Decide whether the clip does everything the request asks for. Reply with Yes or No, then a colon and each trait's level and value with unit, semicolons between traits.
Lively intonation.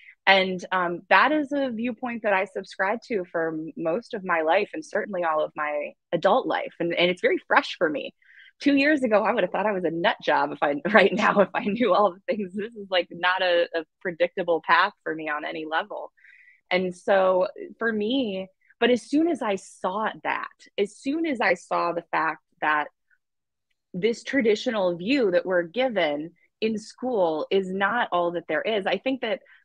Yes: wide, 5.9 semitones